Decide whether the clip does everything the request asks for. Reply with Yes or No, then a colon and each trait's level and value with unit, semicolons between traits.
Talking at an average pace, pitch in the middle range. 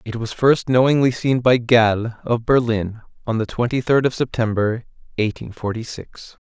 No: average, 165 wpm; low, 120 Hz